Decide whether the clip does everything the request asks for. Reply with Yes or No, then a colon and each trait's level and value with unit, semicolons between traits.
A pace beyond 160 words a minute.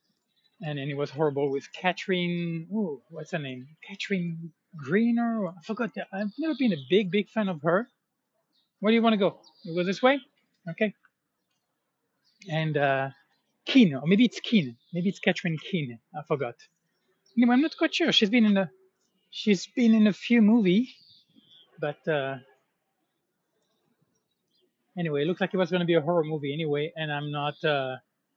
Yes: average, 170 wpm